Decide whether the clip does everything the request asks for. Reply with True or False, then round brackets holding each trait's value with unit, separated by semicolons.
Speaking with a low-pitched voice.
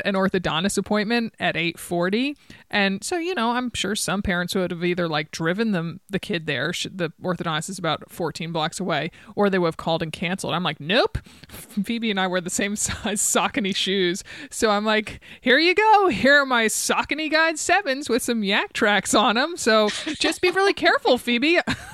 False (205 Hz)